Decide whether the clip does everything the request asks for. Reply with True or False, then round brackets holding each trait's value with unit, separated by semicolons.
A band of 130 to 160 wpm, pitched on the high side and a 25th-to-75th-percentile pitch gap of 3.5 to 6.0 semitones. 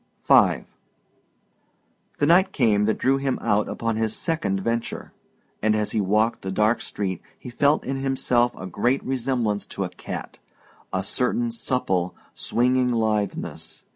False (145 wpm; 115 Hz; 4.0 semitones)